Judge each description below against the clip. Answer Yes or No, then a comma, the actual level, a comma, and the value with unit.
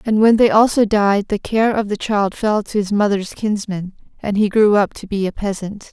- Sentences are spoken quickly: Yes, fast, 235 wpm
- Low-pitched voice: No, high, 205 Hz